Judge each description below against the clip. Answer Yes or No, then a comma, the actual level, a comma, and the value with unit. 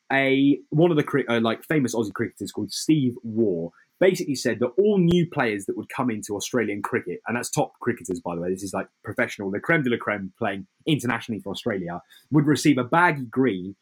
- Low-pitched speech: Yes, low, 125 Hz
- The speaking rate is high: Yes, fast, 215 wpm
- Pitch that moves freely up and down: Yes, wide, 6.6 semitones